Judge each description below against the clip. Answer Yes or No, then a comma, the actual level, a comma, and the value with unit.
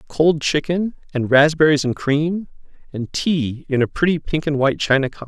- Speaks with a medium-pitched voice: Yes, medium, 150 Hz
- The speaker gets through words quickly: No, average, 180 wpm